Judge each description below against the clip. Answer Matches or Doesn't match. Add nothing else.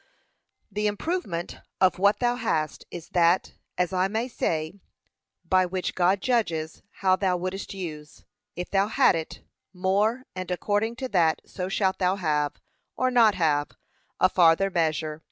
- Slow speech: Doesn't match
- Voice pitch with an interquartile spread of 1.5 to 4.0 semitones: Matches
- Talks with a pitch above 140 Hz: Matches